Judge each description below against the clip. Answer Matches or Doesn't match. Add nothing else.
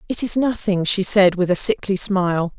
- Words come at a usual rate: Doesn't match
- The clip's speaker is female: Matches